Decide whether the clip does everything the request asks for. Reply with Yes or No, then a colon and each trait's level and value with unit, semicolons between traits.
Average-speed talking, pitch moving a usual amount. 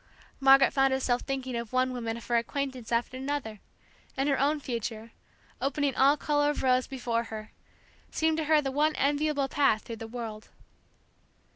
Yes: average, 170 wpm; average, 3.3 semitones